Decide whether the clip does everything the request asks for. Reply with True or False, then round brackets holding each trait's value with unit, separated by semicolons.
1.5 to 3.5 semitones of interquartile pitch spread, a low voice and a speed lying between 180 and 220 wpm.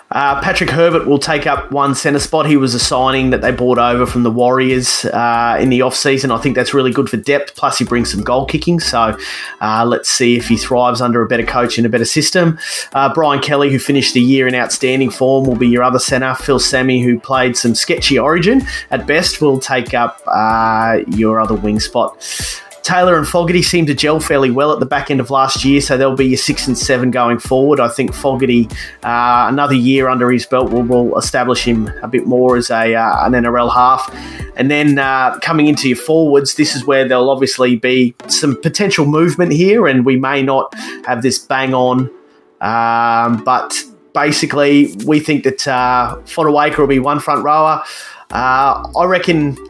True (2.8 semitones; 130 Hz; 205 wpm)